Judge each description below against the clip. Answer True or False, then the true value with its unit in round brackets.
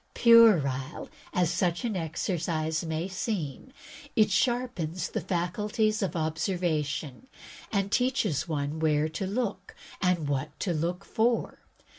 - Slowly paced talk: True (120 wpm)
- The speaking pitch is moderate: True (175 Hz)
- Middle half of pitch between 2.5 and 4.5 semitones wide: False (5.0 semitones)